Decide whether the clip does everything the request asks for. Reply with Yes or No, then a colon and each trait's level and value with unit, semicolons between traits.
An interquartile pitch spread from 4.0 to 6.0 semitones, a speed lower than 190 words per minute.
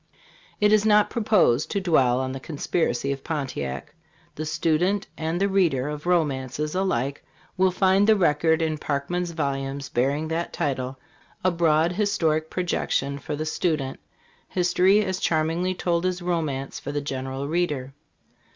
Yes: average, 4.4 semitones; average, 155 wpm